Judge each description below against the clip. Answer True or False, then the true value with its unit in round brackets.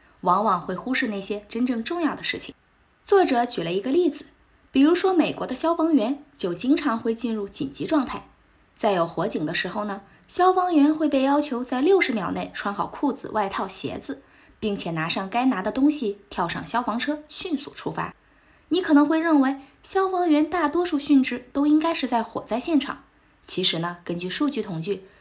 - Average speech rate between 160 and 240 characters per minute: False (285 characters per minute)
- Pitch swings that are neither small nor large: False (6.5 semitones)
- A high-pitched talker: True (270 Hz)